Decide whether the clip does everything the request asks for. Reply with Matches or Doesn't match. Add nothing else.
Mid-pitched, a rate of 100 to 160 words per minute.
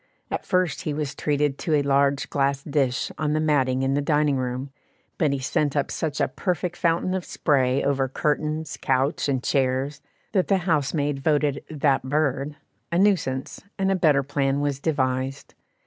Doesn't match